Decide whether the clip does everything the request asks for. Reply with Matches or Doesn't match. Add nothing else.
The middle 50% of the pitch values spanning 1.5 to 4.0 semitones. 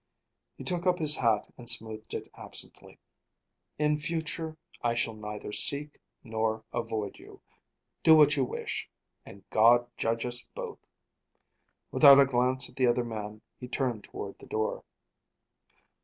Doesn't match